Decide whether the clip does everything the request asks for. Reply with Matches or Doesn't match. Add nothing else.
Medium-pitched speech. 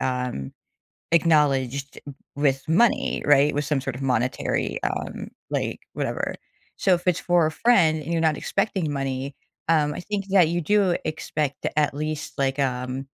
Matches